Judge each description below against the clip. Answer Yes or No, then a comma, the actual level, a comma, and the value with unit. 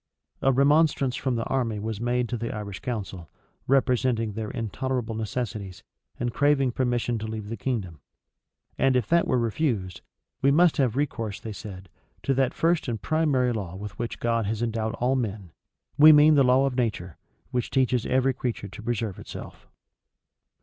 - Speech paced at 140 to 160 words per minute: No, average, 170 wpm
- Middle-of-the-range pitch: No, low, 120 Hz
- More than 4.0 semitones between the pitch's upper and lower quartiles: No, average, 3.5 semitones